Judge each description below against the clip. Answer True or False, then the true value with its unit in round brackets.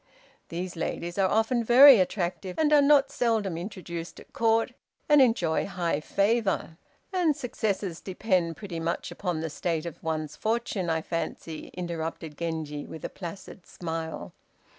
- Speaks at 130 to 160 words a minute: True (145 wpm)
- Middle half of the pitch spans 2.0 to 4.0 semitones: False (5.3 semitones)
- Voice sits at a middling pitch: True (180 Hz)